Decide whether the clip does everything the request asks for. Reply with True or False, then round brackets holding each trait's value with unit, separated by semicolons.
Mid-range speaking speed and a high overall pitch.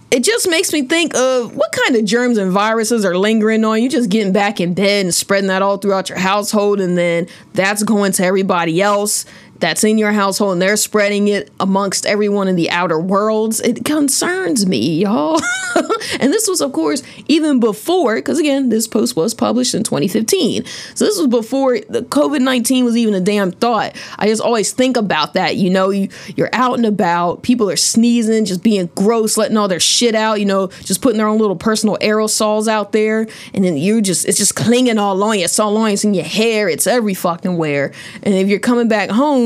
False (215 wpm; 215 Hz)